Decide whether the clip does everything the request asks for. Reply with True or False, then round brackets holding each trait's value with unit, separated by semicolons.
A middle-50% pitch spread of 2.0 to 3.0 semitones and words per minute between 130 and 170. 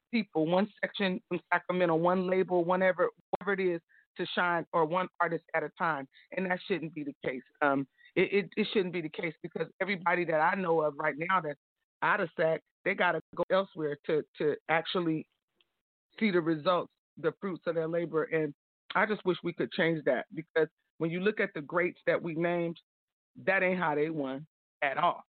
False (2.6 semitones; 200 wpm)